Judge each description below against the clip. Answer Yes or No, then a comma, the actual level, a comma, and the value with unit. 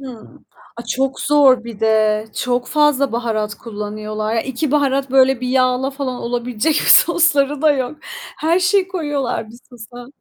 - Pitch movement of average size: Yes, average, 3.8 semitones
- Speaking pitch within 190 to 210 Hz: No, very high, 255 Hz